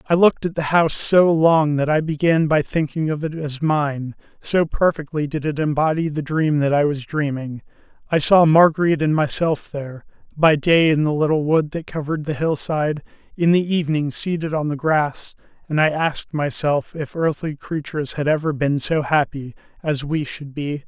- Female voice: No, male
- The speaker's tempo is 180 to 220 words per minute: Yes, average, 190 wpm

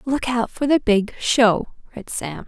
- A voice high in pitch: Yes, high, 235 Hz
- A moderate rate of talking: Yes, average, 195 wpm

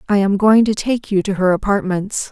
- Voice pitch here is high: Yes, high, 200 Hz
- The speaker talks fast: Yes, fast, 235 wpm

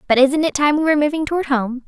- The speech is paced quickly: Yes, fast, 290 wpm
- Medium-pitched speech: No, very high, 285 Hz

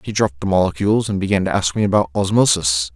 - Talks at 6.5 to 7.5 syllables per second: Yes, 6.8 syllables/s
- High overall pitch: No, very low, 95 Hz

